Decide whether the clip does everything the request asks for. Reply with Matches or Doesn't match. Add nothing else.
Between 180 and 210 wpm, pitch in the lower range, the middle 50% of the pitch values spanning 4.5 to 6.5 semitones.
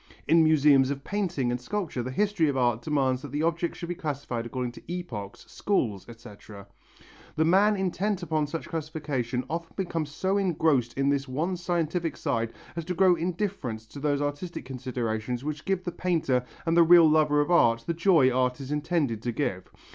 Doesn't match